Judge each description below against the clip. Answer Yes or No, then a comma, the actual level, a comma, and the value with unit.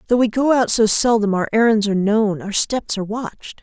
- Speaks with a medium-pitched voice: No, high, 215 Hz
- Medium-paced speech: No, fast, 230 wpm